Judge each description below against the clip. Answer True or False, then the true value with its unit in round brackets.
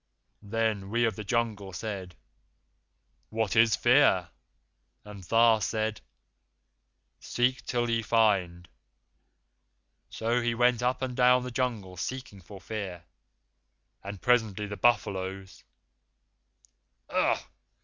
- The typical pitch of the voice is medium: False (110 Hz)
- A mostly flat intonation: False (3.5 semitones)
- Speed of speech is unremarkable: False (110 wpm)